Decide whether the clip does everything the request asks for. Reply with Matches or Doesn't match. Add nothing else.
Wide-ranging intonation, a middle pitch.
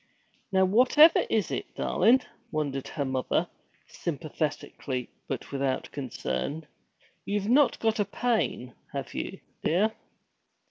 Matches